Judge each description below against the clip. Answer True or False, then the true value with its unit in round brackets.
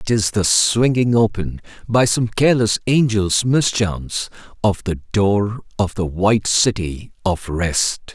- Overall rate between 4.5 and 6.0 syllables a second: False (4.0 syllables/s)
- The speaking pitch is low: True (105 Hz)